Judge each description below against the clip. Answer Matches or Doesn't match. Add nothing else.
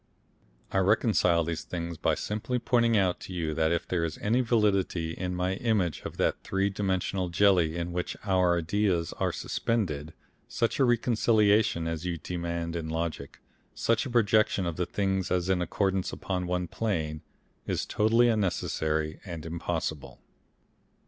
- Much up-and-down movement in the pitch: Doesn't match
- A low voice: Matches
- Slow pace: Doesn't match